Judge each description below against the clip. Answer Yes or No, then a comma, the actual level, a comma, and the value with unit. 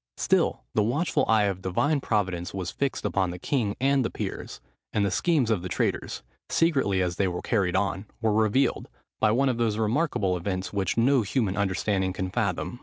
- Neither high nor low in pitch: No, low, 105 Hz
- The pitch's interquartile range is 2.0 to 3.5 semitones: No, average, 4.5 semitones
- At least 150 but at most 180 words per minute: No, average, 190 wpm